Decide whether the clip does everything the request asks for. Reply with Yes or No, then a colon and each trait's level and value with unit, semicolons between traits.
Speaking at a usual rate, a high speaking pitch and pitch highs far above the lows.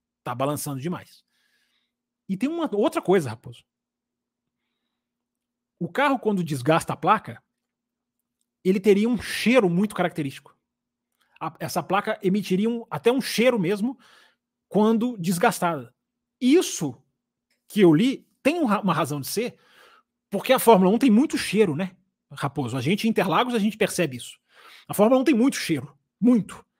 Yes: average, 145 wpm; high, 200 Hz; wide, 6.2 semitones